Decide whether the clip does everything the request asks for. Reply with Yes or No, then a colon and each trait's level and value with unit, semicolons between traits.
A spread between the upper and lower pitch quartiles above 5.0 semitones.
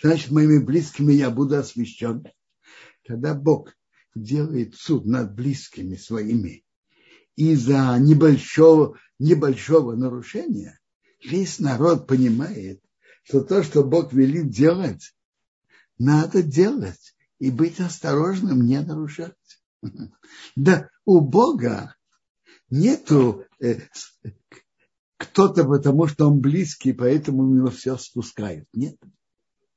No: average, 4.1 semitones